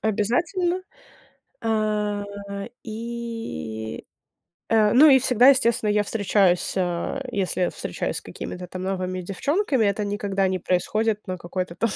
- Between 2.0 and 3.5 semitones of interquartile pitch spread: No, average, 3.9 semitones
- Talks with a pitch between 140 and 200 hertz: No, high, 210 Hz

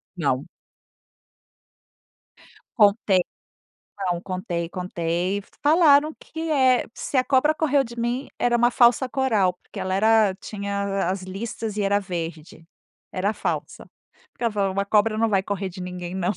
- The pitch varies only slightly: No, average, 4.3 semitones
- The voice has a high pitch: Yes, high, 205 Hz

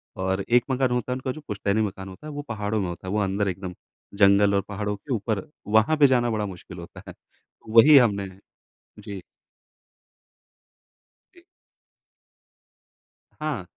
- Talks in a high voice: No, low, 105 Hz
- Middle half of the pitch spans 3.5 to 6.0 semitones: Yes, average, 4.1 semitones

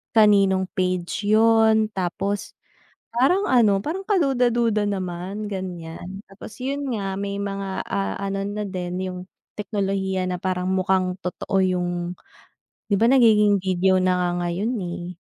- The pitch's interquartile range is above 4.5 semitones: No, average, 2.7 semitones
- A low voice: No, high, 195 Hz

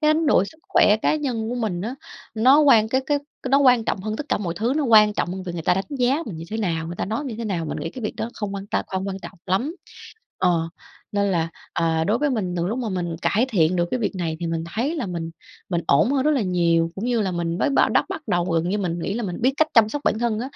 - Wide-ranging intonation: Yes, wide, 5.9 semitones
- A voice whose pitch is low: No, high, 210 Hz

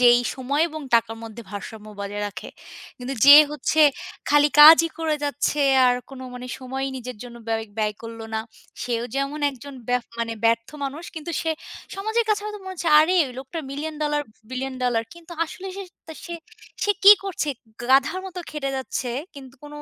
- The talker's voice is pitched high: Yes, very high, 275 Hz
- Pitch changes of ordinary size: Yes, average, 4.6 semitones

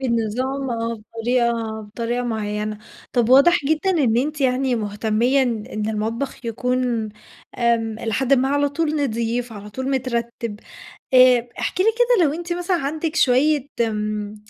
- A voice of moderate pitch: No, high, 245 Hz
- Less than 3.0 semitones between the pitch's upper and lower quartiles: No, average, 3.7 semitones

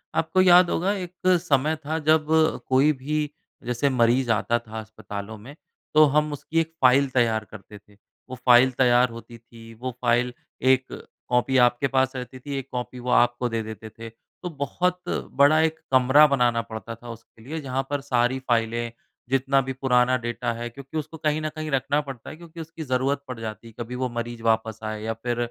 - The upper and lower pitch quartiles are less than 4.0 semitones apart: Yes, average, 3.4 semitones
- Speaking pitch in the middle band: No, low, 125 Hz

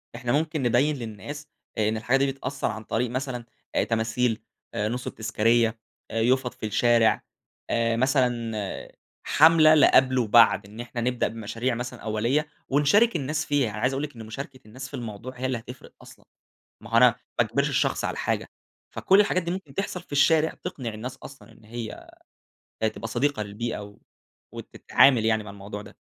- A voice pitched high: No, low, 120 Hz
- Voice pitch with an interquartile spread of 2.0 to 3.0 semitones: No, average, 3.6 semitones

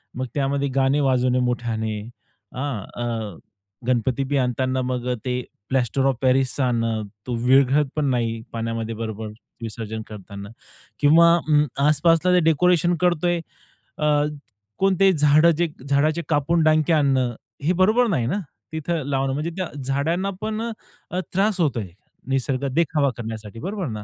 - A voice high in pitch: No, low, 135 Hz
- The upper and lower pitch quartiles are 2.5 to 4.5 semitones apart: No, average, 5.0 semitones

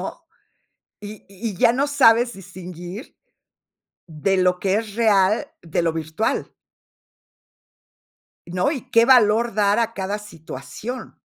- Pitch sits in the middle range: No, high, 205 Hz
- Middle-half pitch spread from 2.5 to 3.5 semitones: No, average, 4.1 semitones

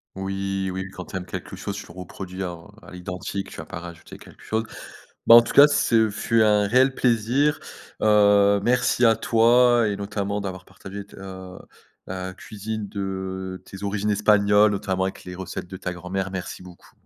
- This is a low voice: Yes, low, 100 Hz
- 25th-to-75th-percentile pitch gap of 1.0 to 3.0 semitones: Yes, narrow, 2.4 semitones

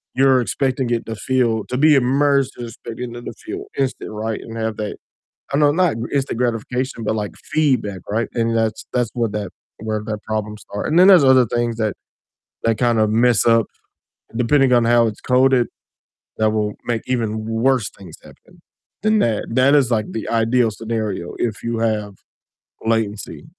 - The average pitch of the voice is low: Yes, low, 115 Hz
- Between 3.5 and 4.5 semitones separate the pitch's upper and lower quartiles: No, average, 2.8 semitones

